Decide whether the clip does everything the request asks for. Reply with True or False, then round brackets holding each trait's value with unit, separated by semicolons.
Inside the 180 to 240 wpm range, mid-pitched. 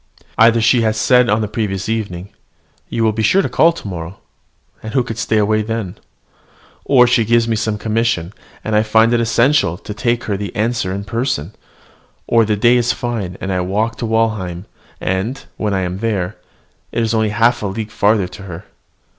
False (200 wpm; 110 Hz)